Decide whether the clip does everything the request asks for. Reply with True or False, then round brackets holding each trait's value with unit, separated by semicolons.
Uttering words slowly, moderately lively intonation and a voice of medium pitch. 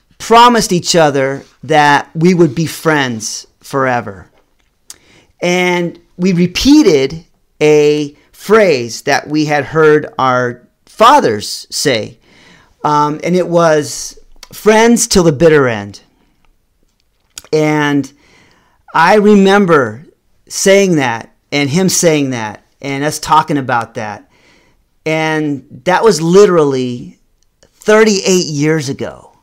True (105 wpm; 4.3 semitones; 155 Hz)